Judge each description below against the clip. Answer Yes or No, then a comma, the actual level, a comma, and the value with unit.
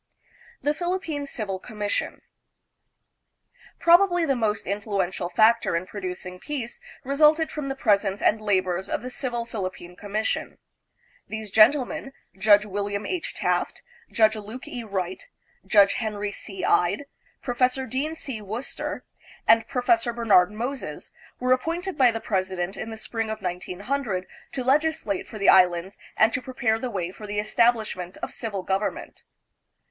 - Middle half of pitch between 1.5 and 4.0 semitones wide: No, average, 4.6 semitones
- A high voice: Yes, high, 220 Hz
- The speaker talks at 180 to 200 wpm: No, average, 145 wpm